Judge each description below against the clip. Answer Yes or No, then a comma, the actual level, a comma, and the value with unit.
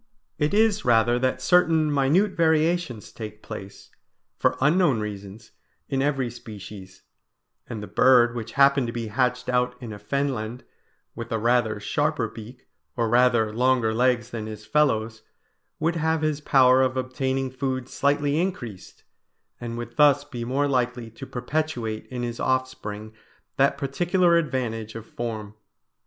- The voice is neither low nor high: No, low, 125 Hz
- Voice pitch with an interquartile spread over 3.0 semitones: Yes, average, 4.1 semitones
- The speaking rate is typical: Yes, average, 145 wpm